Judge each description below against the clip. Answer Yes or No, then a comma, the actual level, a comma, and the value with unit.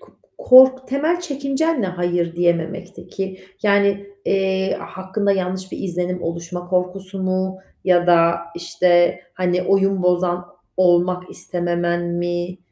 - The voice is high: No, medium, 180 Hz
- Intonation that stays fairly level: Yes, narrow, 1.9 semitones